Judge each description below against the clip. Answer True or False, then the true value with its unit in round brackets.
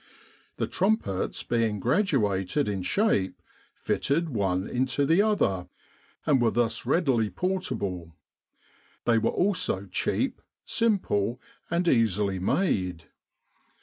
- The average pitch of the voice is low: True (115 Hz)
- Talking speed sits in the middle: False (105 wpm)